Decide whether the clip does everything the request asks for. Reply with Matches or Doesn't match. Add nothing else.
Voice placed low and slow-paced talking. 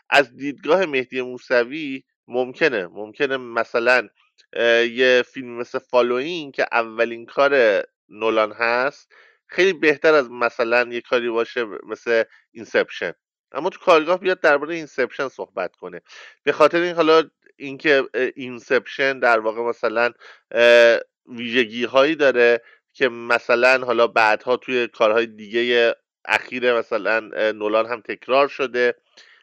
Matches